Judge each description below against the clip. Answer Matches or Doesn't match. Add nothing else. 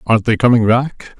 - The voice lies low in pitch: Matches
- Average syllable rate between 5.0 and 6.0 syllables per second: Matches